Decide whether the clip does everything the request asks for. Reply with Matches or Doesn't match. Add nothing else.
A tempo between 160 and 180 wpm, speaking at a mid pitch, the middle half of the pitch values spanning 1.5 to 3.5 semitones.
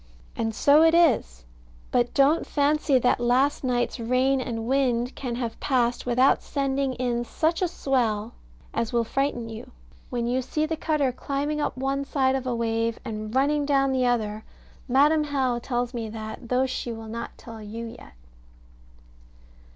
Doesn't match